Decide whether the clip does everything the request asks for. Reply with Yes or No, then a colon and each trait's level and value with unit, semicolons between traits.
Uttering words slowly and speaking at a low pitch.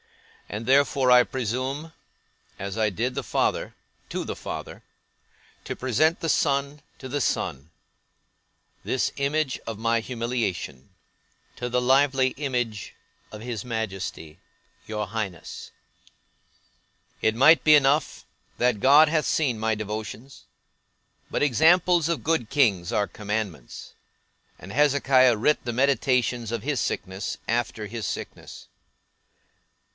Yes: slow, 120 wpm; low, 125 Hz